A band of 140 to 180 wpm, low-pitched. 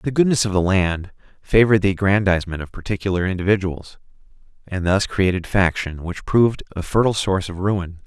Yes: average, 165 wpm; very low, 95 Hz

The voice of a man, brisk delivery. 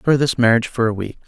Yes: male; fast, 285 wpm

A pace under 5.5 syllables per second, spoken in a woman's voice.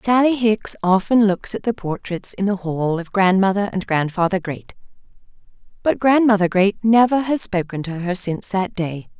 Yes: 4.9 syllables/s; female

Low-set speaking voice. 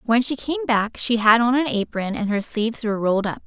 No: high, 230 Hz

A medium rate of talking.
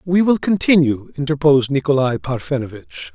No: slow, 115 wpm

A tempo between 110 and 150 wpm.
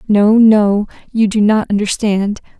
Yes: average, 140 wpm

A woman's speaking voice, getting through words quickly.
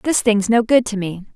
Yes: female; fast, 265 wpm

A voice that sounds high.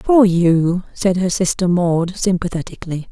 No: medium, 180 Hz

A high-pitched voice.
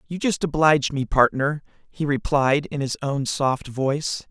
No: medium, 145 Hz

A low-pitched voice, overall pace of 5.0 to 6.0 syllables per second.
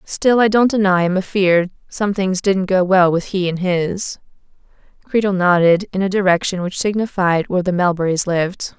No: medium, 185 Hz; 5.1 syllables/s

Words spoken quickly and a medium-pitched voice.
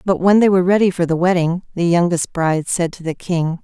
Yes: fast, 250 wpm; medium, 175 Hz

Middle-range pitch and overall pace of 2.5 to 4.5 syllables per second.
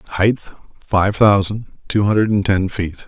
No: low, 100 Hz; 4.4 syllables/s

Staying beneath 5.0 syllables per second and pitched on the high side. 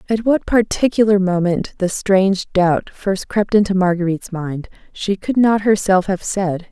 Yes: 4.5 syllables/s; high, 195 Hz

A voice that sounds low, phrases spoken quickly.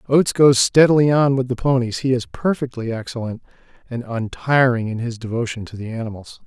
No: low, 125 Hz; average, 165 wpm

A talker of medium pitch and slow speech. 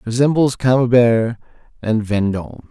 No: low, 120 Hz; slow, 90 wpm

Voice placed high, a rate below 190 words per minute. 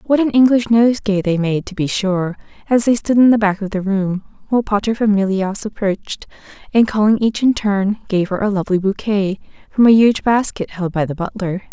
No: high, 205 Hz; average, 200 wpm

